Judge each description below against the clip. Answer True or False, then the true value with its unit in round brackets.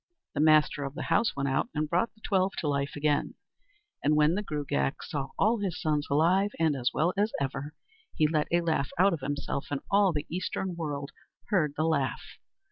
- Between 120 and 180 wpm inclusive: False (205 wpm)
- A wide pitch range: False (3.8 semitones)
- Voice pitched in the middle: True (155 Hz)